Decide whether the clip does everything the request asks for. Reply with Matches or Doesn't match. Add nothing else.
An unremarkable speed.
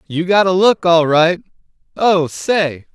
Matches